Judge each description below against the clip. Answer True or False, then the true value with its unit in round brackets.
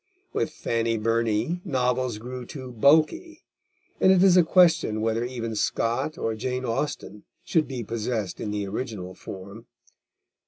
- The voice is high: False (120 Hz)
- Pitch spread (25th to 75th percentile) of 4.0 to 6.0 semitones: True (4.8 semitones)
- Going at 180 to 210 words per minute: False (145 wpm)